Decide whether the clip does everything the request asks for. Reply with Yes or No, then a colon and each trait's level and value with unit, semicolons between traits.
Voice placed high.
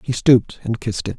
No: low, 115 Hz